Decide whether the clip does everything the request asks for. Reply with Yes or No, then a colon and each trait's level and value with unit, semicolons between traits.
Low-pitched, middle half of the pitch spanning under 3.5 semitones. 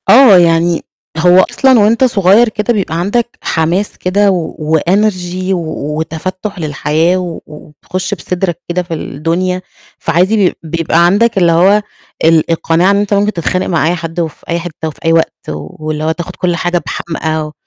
No: medium, 175 Hz; average, 2.9 semitones